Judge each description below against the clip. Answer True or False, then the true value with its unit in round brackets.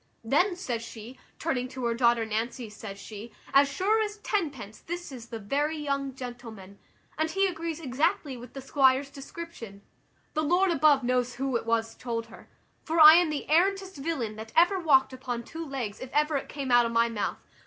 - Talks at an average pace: True (195 wpm)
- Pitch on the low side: False (270 Hz)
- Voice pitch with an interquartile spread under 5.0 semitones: False (5.4 semitones)